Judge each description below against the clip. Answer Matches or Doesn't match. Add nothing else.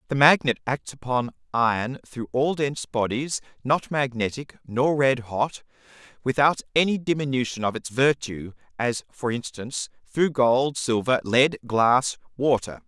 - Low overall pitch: Matches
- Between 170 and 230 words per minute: Doesn't match